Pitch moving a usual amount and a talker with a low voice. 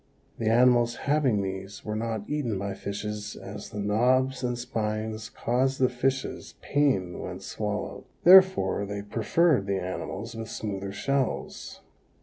Yes: average, 4.1 semitones; low, 115 Hz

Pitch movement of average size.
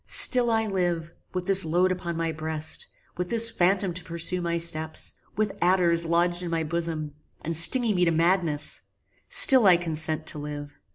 No: narrow, 2.3 semitones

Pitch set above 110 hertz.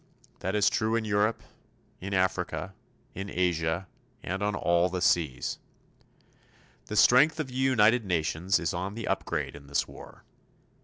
No: very low, 95 Hz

